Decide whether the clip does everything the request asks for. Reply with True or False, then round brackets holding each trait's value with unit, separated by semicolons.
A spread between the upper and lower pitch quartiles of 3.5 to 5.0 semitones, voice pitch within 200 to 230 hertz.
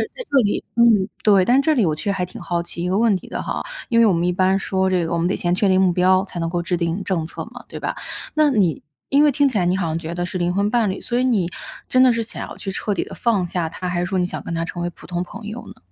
False (3.8 semitones; 185 Hz)